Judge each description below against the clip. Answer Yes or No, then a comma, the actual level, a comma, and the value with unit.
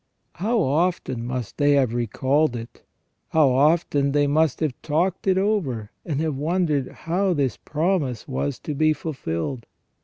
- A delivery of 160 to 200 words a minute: No, average, 150 wpm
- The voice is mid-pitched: Yes, medium, 145 Hz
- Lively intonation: No, average, 4.3 semitones